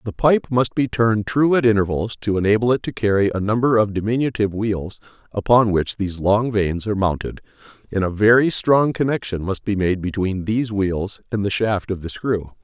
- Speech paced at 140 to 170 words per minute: No, average, 200 wpm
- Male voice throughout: Yes, male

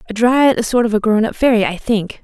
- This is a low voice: No, high, 225 Hz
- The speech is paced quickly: Yes, fast, 295 wpm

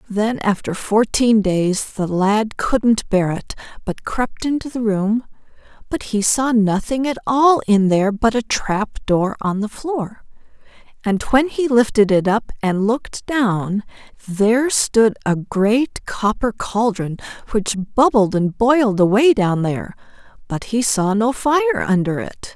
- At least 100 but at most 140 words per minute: No, average, 155 wpm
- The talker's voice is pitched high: Yes, high, 220 Hz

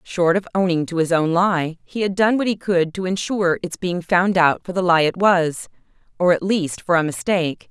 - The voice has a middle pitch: Yes, medium, 175 Hz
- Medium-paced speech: No, fast, 225 wpm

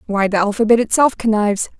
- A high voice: Yes, high, 215 Hz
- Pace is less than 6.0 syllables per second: No, 6.4 syllables/s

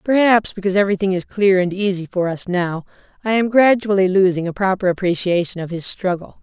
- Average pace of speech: Yes, average, 185 wpm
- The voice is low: No, high, 190 Hz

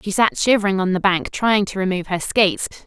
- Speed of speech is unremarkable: No, fast, 230 wpm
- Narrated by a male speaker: No, female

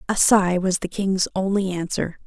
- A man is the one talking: No, female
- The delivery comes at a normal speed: Yes, average, 185 wpm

